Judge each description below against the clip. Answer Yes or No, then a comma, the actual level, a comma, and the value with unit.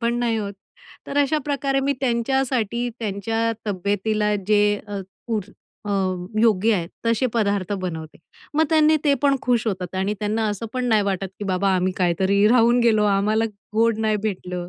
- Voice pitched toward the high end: Yes, high, 215 Hz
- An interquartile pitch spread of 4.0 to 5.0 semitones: No, average, 3.3 semitones